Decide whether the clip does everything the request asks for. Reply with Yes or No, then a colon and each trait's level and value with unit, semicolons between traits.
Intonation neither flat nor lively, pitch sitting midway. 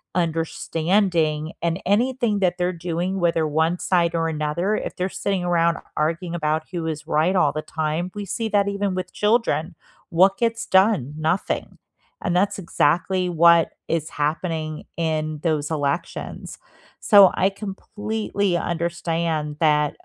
Yes: average, 3.3 semitones; medium, 170 Hz